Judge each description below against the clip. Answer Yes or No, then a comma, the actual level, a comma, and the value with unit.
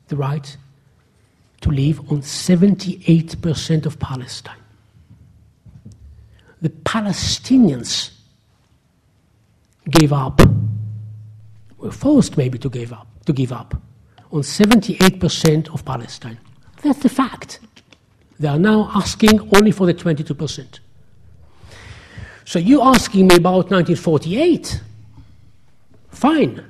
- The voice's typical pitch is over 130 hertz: Yes, medium, 140 Hz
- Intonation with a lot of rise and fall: Yes, wide, 8.1 semitones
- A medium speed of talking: No, slow, 100 wpm